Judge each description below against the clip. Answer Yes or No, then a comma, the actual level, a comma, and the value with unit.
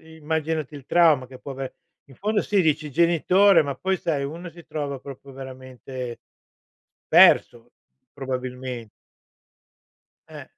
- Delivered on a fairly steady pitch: No, average, 3.9 semitones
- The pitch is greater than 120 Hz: Yes, medium, 140 Hz